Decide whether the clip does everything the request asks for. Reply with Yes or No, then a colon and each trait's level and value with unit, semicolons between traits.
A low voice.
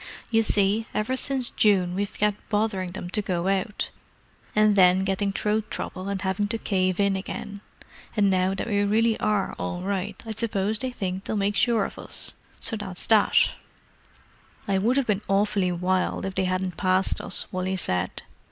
No: high, 200 Hz